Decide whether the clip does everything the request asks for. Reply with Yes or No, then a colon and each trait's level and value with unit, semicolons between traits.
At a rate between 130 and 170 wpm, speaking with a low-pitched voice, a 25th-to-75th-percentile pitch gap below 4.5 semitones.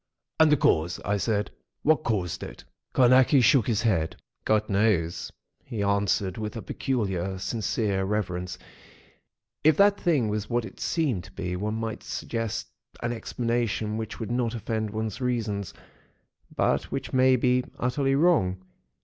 Yes: average, 150 wpm; low, 110 Hz; average, 3.8 semitones